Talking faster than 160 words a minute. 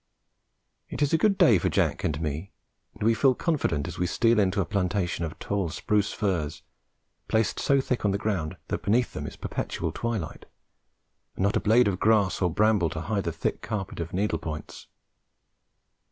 Yes: average, 190 wpm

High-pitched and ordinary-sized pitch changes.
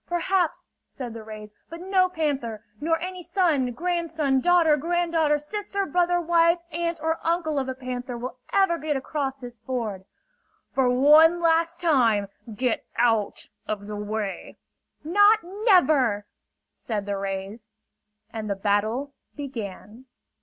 No: very high, 285 Hz; wide, 7.0 semitones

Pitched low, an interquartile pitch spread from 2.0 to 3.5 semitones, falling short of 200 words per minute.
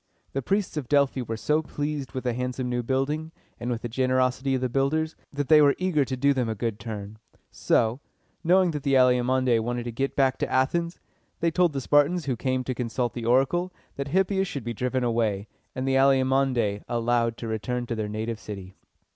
No: low, 130 Hz; average, 3.1 semitones; fast, 205 wpm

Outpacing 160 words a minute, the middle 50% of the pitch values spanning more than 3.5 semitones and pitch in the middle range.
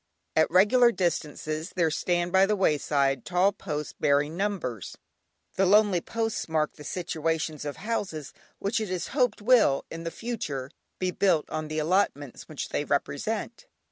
No: average, 155 wpm; average, 5.0 semitones; medium, 170 Hz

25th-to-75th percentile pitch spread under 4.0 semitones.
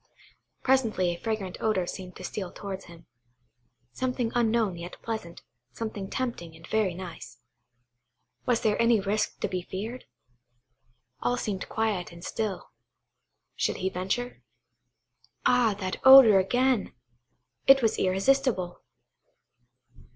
No: average, 4.4 semitones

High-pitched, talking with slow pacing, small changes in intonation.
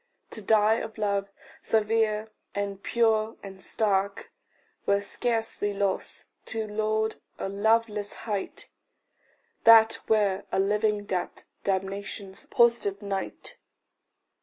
Yes: high, 210 Hz; slow, 105 wpm; narrow, 1.8 semitones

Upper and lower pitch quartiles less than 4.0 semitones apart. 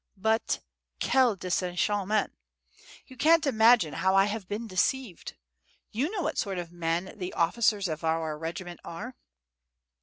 No: average, 5.0 semitones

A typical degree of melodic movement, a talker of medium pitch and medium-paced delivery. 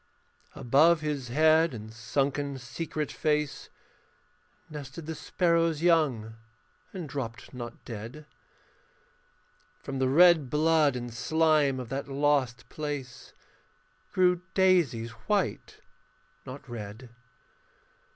No: average, 4.2 semitones; medium, 145 Hz; slow, 100 wpm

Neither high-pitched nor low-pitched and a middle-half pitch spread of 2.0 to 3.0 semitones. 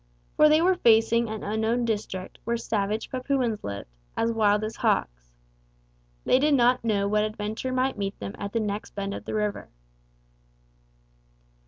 No: high, 220 Hz; average, 2.7 semitones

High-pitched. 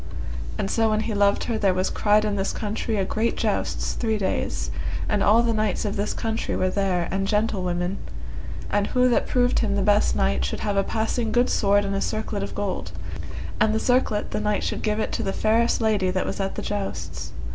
Yes: high, 205 Hz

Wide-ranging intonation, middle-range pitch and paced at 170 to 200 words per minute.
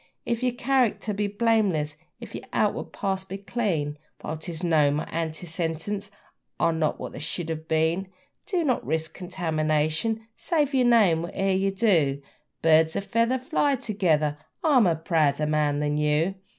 No: wide, 5.7 semitones; medium, 175 Hz; average, 160 wpm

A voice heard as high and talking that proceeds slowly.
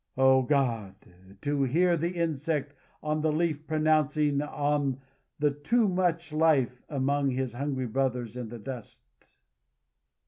No: medium, 145 Hz; slow, 130 wpm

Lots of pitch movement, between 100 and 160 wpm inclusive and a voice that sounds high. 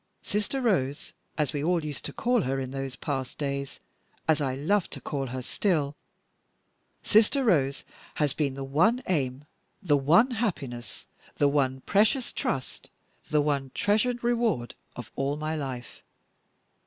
No: wide, 7.1 semitones; average, 150 wpm; medium, 145 Hz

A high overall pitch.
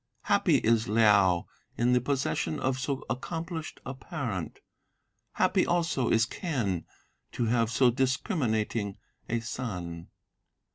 No: low, 120 Hz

